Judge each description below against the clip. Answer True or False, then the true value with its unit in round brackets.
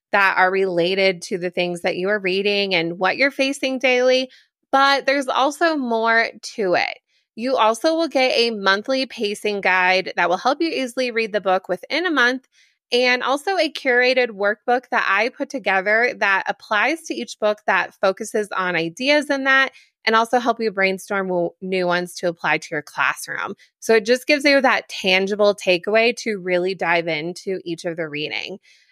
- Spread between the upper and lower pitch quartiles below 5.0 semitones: False (5.6 semitones)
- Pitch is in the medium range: False (215 Hz)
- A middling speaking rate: True (185 wpm)